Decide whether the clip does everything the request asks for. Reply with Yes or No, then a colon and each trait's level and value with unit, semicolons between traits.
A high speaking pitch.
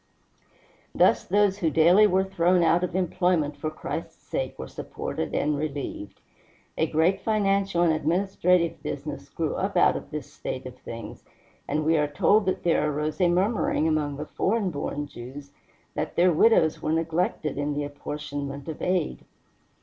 No: medium, 160 Hz